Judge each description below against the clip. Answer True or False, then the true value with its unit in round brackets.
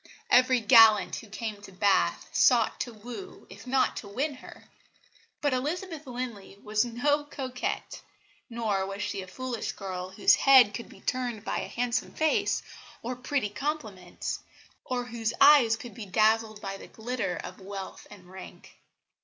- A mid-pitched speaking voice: False (230 Hz)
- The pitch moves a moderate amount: True (3.9 semitones)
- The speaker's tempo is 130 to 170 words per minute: True (160 wpm)